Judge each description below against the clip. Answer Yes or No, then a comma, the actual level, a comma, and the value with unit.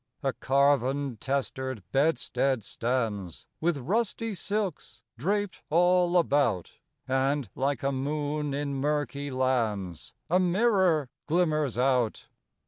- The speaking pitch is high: No, medium, 140 Hz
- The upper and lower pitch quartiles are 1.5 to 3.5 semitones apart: No, average, 4.2 semitones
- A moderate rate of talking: No, slow, 105 wpm